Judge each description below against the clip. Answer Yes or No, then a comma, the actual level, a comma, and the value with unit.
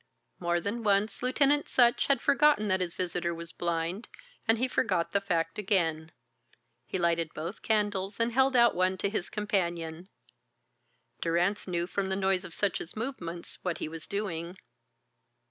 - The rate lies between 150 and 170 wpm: Yes, average, 160 wpm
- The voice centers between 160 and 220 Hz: Yes, high, 190 Hz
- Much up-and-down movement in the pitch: No, average, 3.9 semitones